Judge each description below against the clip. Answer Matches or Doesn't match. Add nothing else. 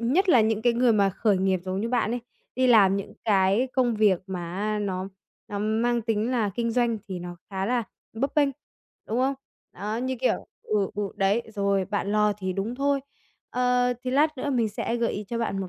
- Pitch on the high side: Matches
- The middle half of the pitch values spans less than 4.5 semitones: Matches